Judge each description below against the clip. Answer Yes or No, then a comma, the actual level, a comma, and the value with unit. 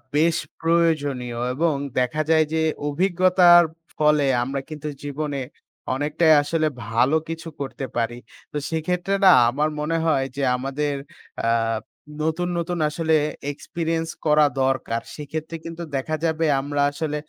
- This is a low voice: No, medium, 155 Hz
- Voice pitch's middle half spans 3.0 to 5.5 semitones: No, narrow, 2.6 semitones